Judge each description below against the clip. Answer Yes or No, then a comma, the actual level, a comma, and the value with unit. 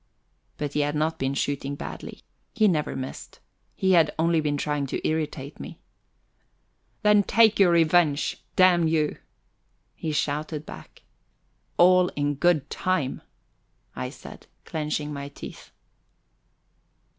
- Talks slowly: Yes, slow, 125 wpm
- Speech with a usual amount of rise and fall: Yes, average, 3.2 semitones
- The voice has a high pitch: No, medium, 155 Hz